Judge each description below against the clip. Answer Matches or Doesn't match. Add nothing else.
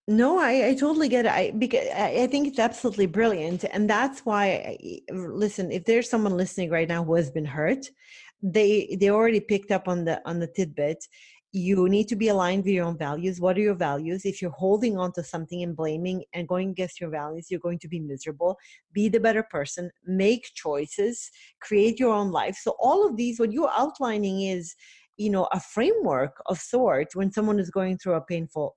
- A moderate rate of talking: Doesn't match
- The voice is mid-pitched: Doesn't match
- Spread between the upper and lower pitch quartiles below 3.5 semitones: Doesn't match